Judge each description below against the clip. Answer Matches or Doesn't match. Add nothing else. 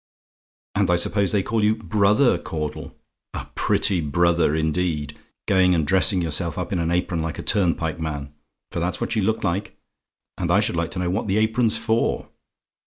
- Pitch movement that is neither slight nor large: Matches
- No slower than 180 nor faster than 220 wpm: Matches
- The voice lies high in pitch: Doesn't match